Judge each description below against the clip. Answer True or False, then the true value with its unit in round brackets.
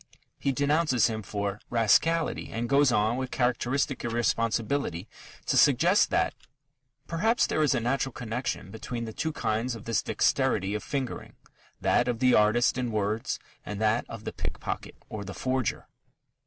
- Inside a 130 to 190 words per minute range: True (155 wpm)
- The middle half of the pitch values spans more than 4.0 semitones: False (3.3 semitones)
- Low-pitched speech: True (120 Hz)